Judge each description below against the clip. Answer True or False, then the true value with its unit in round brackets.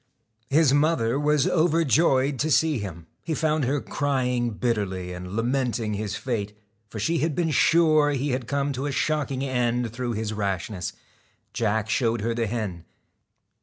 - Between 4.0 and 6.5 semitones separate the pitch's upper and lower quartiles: True (5.0 semitones)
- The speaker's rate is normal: True (160 wpm)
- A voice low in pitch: True (125 Hz)